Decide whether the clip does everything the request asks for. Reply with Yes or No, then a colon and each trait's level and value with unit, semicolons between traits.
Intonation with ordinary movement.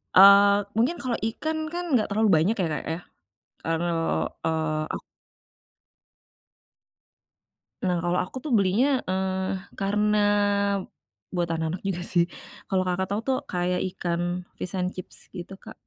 Yes: average, 3.4 semitones